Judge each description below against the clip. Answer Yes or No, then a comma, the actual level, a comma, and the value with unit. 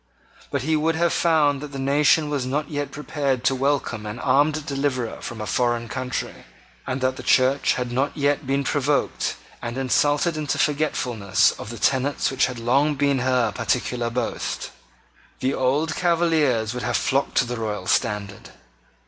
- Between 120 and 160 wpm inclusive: No, average, 170 wpm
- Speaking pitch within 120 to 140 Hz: Yes, low, 135 Hz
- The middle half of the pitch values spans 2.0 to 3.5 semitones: Yes, average, 3.1 semitones